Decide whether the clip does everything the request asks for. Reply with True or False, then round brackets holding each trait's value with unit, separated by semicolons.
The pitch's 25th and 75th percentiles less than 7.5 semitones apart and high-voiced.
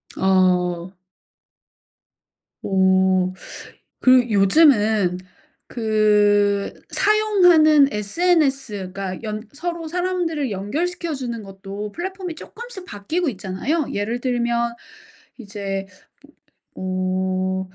False (8.3 semitones; 215 Hz)